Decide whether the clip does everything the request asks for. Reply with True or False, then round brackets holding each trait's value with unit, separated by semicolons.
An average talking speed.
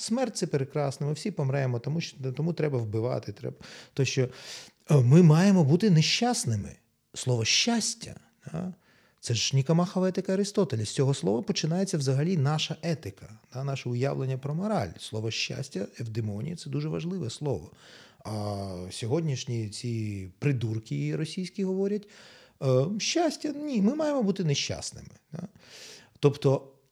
True (130 wpm)